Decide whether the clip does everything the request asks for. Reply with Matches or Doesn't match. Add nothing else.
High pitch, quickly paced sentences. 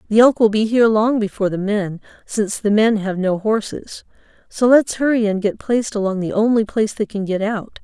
Matches